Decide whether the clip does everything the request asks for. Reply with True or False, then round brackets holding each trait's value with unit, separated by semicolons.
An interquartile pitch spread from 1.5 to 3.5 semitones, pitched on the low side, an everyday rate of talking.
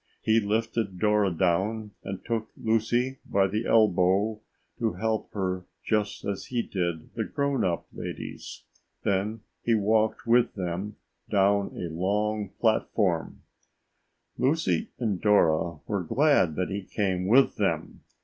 False (3.2 semitones; 105 Hz; 130 wpm)